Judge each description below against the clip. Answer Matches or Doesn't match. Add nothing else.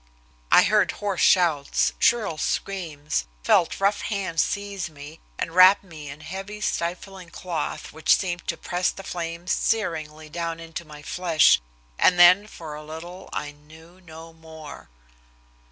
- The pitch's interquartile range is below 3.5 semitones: Matches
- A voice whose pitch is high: Doesn't match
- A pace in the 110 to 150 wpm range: Matches